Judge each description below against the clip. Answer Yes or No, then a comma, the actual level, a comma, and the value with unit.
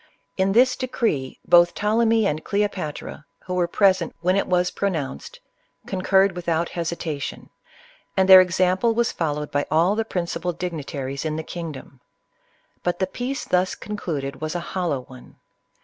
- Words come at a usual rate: Yes, average, 150 wpm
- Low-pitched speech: No, medium, 180 Hz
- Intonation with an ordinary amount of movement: Yes, average, 3.8 semitones